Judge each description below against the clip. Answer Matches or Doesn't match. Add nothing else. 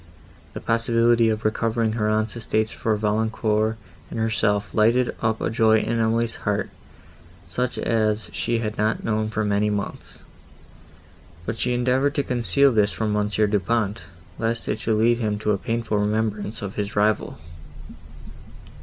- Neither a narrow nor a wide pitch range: Doesn't match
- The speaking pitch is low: Matches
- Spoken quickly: Doesn't match